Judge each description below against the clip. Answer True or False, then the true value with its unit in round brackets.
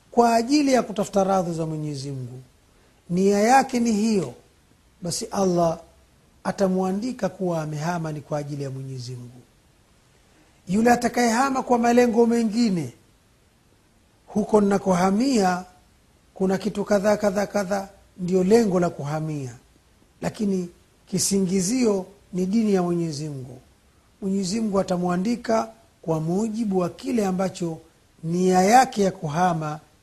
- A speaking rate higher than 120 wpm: False (110 wpm)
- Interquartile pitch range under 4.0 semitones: False (5.2 semitones)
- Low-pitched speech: False (190 Hz)